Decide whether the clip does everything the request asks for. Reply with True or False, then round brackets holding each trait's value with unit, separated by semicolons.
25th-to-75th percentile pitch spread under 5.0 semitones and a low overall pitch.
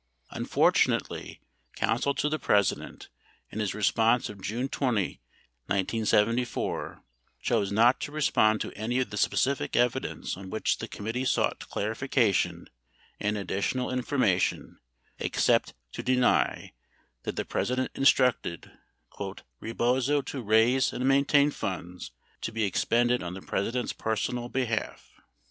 True (3.6 semitones; 115 Hz)